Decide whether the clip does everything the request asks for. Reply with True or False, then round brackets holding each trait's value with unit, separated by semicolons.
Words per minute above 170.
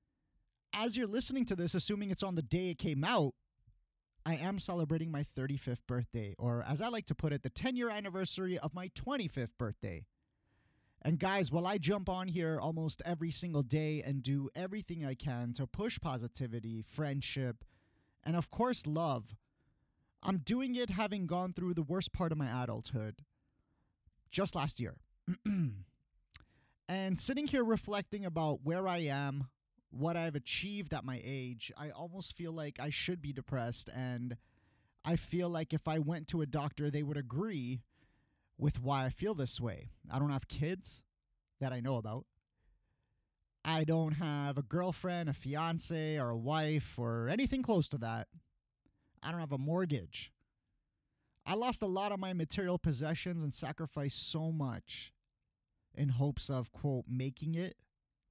False (165 wpm)